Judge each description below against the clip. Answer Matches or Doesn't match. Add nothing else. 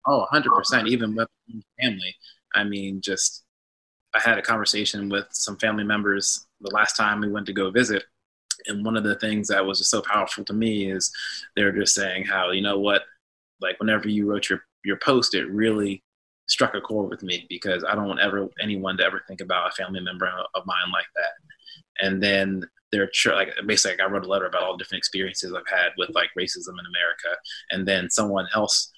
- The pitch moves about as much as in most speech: Doesn't match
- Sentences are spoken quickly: Matches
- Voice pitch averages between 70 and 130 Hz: Matches